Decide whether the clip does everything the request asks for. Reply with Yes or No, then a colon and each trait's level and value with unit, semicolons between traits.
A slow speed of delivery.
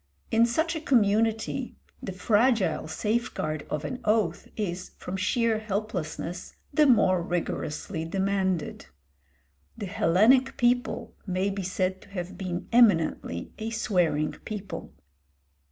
Yes: slow, 120 wpm